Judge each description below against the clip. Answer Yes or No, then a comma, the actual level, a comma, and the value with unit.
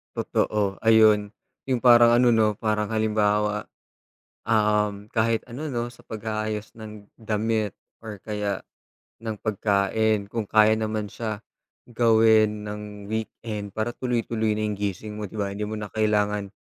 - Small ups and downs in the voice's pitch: Yes, narrow, 1.2 semitones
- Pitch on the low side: Yes, low, 110 Hz